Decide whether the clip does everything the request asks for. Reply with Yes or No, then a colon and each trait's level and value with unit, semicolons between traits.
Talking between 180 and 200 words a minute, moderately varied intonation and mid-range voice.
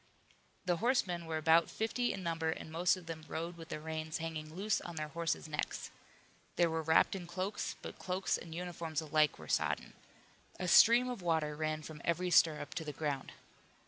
No: average, 190 wpm; narrow, 2.3 semitones; medium, 165 Hz